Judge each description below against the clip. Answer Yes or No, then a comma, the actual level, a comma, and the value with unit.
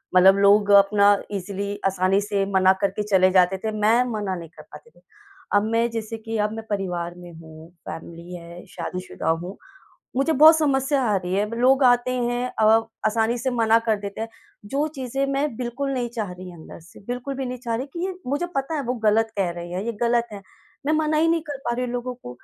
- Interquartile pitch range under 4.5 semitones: No, average, 4.8 semitones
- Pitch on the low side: No, high, 220 Hz